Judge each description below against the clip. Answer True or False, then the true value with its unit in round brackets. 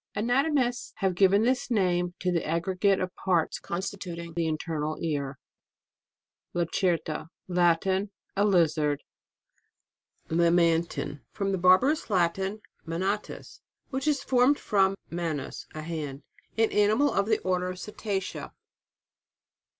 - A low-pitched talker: False (185 Hz)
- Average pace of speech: False (120 wpm)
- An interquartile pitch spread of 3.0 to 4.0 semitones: True (3.5 semitones)